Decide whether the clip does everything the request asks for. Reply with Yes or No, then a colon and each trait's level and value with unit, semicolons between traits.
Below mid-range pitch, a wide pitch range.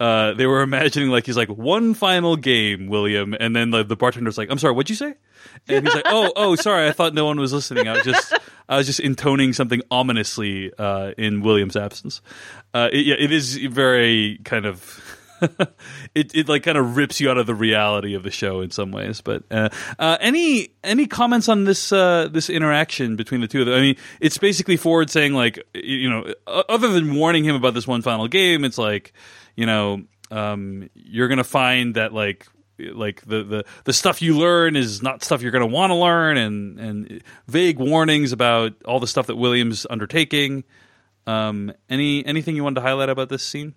Yes: low, 130 Hz; wide, 5.9 semitones